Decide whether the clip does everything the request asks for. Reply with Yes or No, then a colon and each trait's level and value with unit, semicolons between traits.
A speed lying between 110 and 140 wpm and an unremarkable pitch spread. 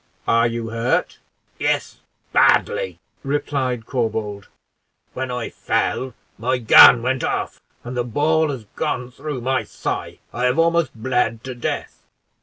Yes: slow, 135 wpm; average, 3.1 semitones